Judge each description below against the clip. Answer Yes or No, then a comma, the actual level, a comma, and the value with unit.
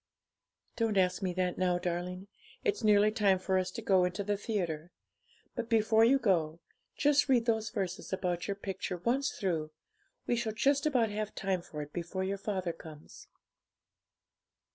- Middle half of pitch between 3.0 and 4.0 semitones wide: Yes, average, 3.6 semitones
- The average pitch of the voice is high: Yes, high, 195 Hz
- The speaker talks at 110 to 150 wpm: No, average, 165 wpm